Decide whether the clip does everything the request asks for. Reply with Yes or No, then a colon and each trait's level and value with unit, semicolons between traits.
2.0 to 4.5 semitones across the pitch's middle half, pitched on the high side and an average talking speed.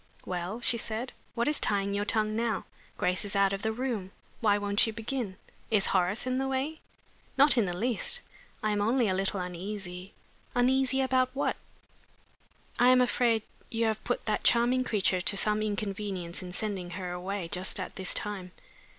Yes: average, 4.1 semitones; high, 210 Hz; average, 185 wpm